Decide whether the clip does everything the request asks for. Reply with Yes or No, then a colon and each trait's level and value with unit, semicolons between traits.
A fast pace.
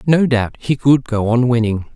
Yes: fast, 215 wpm